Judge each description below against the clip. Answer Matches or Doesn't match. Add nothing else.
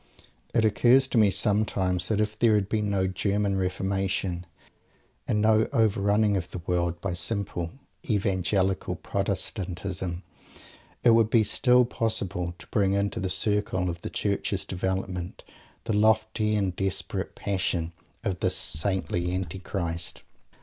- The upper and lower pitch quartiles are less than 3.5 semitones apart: Matches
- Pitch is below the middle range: Matches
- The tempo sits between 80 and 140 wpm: Matches